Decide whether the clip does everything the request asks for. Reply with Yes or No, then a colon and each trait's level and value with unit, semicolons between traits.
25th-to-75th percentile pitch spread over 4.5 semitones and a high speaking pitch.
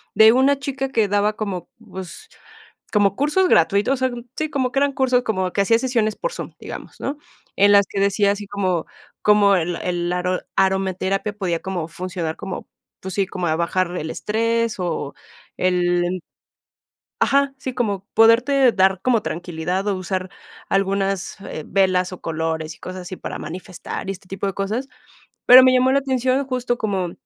Yes: average, 4.9 semitones; high, 195 Hz